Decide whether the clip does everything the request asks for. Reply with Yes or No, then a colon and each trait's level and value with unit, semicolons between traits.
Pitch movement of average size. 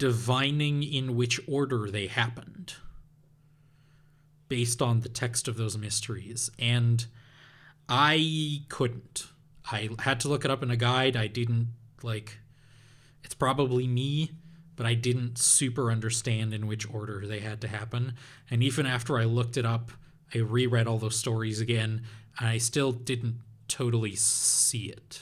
Yes: average, 3.2 semitones